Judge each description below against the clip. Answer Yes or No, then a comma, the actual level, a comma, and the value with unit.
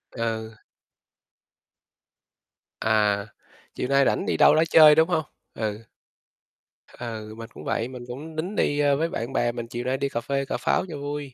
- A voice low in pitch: Yes, low, 130 Hz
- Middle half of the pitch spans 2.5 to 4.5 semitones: Yes, average, 4.2 semitones